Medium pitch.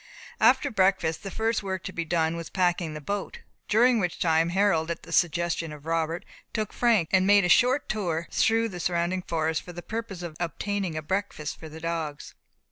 Yes: medium, 175 Hz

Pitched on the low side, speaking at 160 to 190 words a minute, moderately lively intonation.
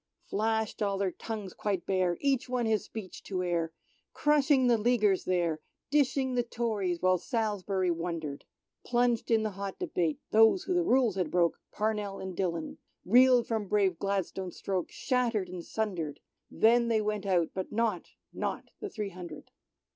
No: high, 205 Hz; average, 170 wpm; average, 4.2 semitones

